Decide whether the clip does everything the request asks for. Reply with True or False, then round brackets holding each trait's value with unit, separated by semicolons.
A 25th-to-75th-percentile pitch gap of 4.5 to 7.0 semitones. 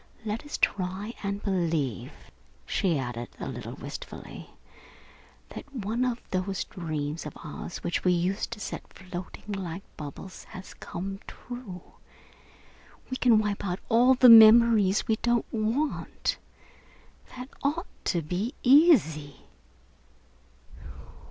True (5.0 semitones)